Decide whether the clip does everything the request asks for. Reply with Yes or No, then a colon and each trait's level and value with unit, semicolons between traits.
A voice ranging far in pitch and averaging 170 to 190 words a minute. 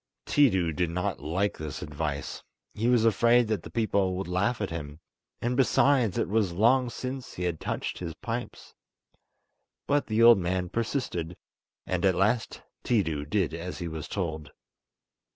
No: wide, 5.7 semitones; average, 150 wpm